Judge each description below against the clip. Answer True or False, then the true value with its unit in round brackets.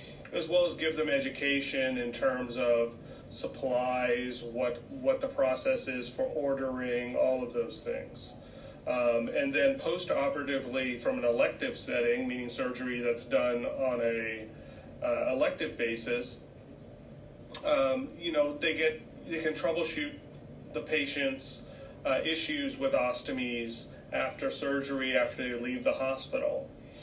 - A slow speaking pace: True (130 wpm)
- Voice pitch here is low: True (130 Hz)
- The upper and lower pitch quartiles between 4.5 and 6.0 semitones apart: True (4.9 semitones)